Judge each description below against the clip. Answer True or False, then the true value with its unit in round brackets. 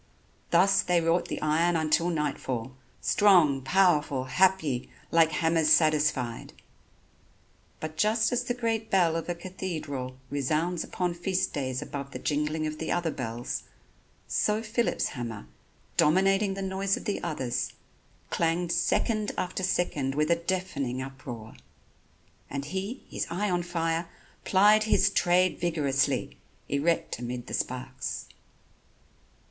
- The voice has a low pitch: False (165 Hz)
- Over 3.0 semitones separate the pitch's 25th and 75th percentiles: True (5.0 semitones)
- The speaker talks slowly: True (130 wpm)